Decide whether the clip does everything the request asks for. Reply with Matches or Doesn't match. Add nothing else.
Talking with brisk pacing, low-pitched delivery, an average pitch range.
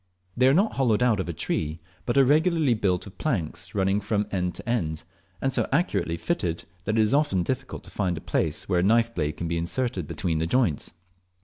Doesn't match